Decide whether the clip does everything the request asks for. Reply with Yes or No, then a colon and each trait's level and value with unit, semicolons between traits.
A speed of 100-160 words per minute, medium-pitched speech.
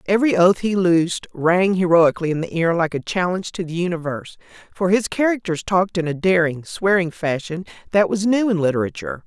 No: average, 190 wpm; medium, 180 Hz